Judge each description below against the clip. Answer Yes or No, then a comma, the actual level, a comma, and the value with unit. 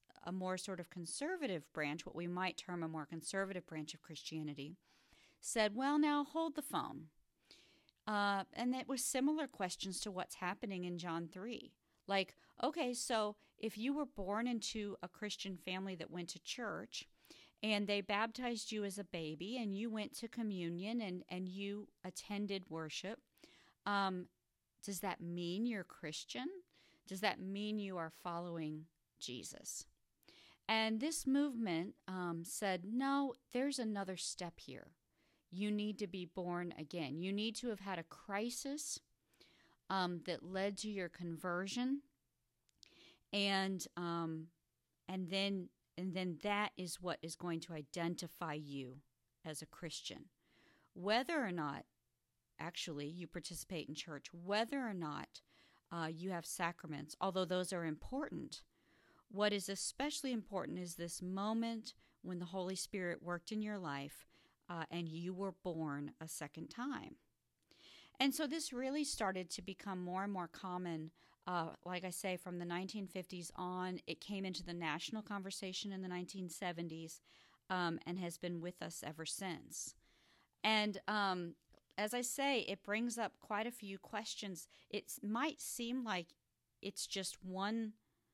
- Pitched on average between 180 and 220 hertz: Yes, medium, 185 Hz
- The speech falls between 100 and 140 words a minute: No, average, 150 wpm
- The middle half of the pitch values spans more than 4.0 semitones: No, average, 3.7 semitones